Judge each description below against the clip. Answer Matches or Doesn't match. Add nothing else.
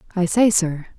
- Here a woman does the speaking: Matches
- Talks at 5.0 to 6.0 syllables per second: Matches